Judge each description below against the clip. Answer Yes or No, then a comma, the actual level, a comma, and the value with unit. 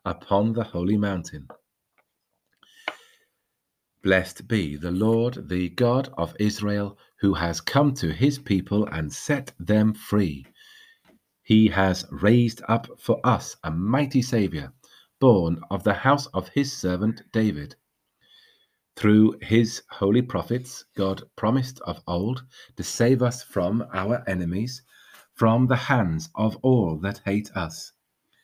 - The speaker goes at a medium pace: No, slow, 130 wpm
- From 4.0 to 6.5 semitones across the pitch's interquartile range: Yes, average, 4.5 semitones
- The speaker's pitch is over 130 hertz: No, low, 105 Hz